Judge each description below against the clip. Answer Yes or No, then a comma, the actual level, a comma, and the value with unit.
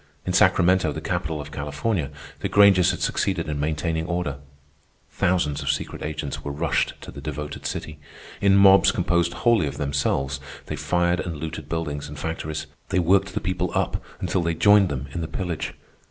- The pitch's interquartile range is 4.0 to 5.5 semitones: No, average, 3.5 semitones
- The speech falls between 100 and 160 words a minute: No, average, 180 wpm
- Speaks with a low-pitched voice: Yes, very low, 80 Hz